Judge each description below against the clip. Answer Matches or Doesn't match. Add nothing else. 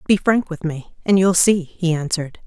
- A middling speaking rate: Doesn't match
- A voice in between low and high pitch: Matches